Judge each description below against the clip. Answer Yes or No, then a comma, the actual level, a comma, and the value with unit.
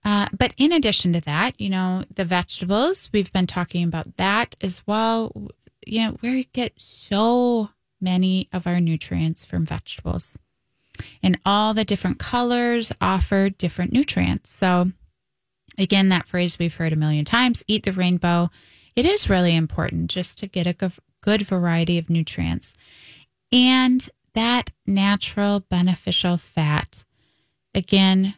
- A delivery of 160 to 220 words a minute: No, slow, 135 wpm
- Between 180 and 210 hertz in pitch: Yes, high, 190 Hz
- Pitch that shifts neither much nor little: Yes, average, 3.8 semitones